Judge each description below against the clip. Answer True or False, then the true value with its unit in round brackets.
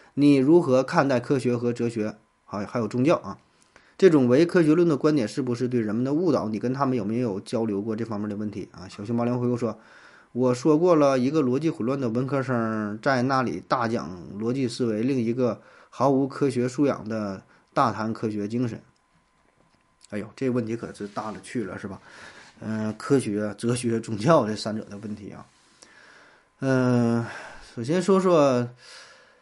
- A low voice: True (120 Hz)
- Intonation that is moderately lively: True (3.5 semitones)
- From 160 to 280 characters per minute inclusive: True (270 characters per minute)